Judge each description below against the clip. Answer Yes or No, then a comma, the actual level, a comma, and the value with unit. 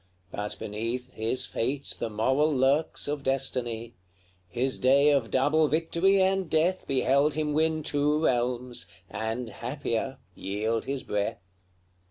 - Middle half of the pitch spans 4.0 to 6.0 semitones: Yes, average, 4.3 semitones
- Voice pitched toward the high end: No, low, 135 Hz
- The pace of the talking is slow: Yes, slow, 130 wpm